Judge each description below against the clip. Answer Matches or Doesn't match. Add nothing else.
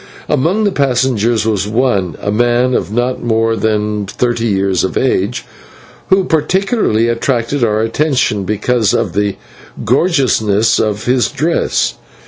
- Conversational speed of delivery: Doesn't match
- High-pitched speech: Doesn't match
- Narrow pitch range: Doesn't match